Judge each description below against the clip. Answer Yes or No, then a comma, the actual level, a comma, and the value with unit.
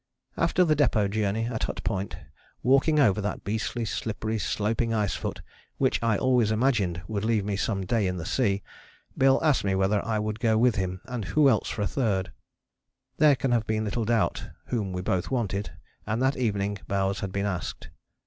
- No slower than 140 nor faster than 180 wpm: No, average, 195 wpm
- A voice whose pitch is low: Yes, low, 110 Hz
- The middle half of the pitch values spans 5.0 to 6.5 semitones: No, average, 3.3 semitones